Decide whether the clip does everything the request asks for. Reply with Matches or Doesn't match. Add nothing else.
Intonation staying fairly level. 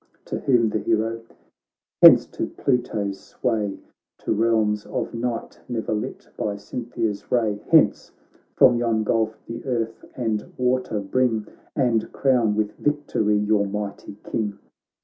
Matches